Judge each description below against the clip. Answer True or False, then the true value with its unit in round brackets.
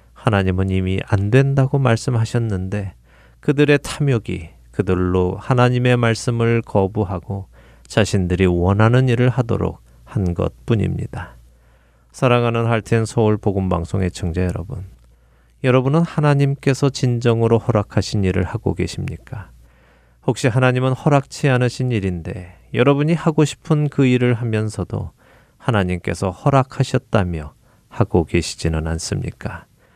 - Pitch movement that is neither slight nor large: False (5.8 semitones)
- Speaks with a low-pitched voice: True (105 Hz)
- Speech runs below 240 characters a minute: False (295 characters per minute)